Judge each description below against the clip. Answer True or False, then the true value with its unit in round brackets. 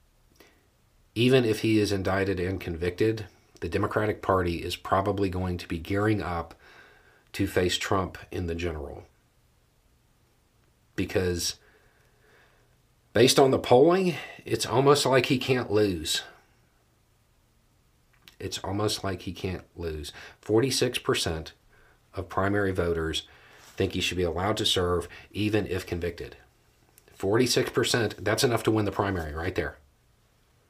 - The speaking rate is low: True (125 wpm)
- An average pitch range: True (3.6 semitones)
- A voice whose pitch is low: True (95 Hz)